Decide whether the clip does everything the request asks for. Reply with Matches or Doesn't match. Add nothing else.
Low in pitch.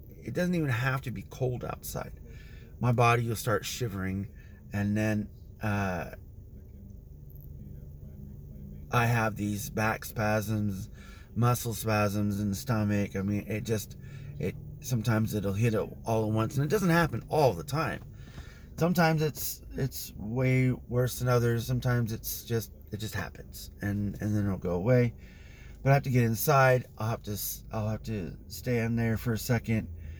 Matches